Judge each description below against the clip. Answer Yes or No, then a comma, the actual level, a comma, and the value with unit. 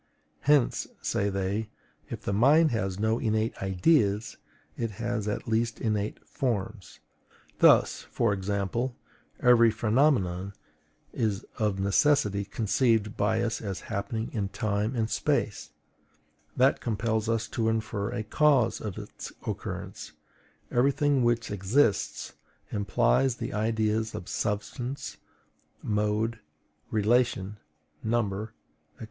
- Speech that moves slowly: Yes, slow, 115 wpm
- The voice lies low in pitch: Yes, low, 110 Hz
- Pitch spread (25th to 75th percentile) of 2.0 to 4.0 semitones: Yes, narrow, 2.6 semitones